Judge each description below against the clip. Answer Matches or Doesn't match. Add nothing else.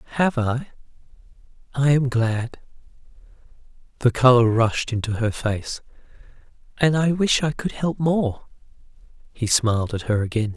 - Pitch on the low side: Matches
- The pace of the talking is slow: Matches